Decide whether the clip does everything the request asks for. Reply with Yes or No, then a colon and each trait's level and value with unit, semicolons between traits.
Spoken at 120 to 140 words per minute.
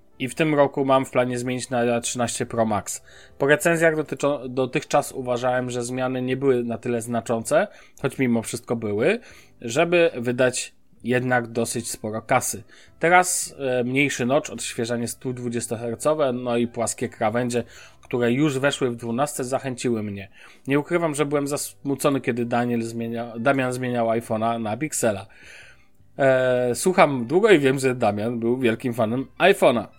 No: average, 150 wpm